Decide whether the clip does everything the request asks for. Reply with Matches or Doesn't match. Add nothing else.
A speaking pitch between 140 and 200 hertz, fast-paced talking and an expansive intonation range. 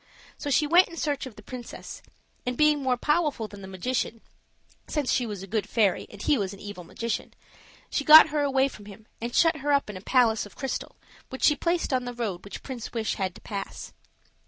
Doesn't match